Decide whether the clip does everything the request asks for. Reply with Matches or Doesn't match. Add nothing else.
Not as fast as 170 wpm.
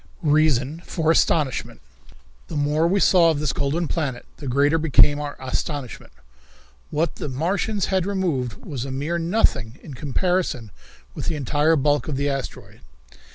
Matches